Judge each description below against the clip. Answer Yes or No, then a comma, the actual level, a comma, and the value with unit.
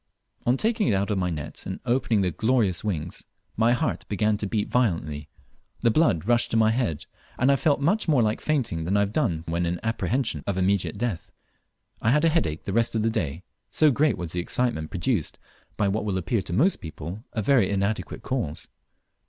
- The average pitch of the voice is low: Yes, low, 105 Hz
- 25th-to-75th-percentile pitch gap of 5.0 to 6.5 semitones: Yes, wide, 5.6 semitones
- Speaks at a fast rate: Yes, fast, 210 wpm